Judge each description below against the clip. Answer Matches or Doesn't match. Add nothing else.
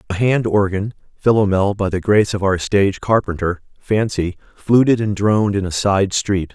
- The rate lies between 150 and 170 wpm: Matches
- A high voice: Doesn't match